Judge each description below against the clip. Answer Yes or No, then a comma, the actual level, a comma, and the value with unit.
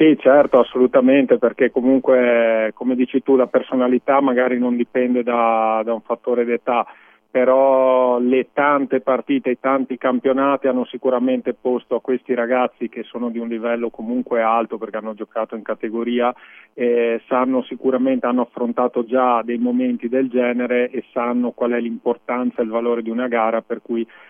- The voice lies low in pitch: Yes, low, 125 Hz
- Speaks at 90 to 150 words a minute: No, average, 165 wpm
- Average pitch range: No, narrow, 1.5 semitones